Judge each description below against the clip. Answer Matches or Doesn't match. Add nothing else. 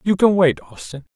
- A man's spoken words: Matches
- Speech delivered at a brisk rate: Matches